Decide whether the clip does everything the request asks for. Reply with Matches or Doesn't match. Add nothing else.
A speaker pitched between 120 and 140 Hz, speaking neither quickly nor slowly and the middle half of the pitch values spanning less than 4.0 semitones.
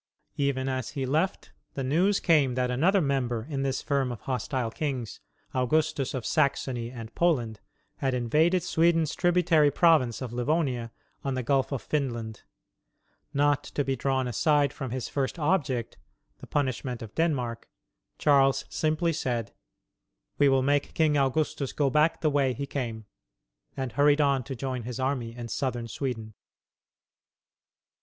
Matches